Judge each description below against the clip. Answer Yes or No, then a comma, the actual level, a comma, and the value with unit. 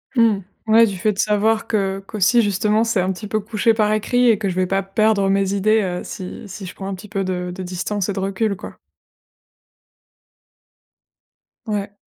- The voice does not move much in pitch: Yes, narrow, 2.1 semitones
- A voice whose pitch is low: No, high, 200 Hz